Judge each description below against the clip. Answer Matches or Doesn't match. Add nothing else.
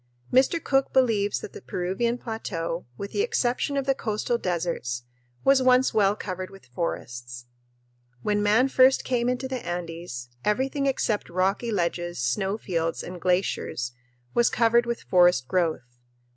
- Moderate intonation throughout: Doesn't match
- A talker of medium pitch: Doesn't match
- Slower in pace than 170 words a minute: Matches